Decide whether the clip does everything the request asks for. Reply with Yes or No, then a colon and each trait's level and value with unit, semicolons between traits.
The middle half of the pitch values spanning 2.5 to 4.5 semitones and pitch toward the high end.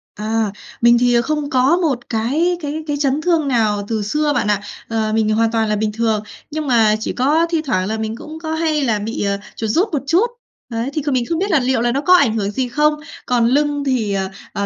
No: wide, 5.4 semitones; very high, 250 Hz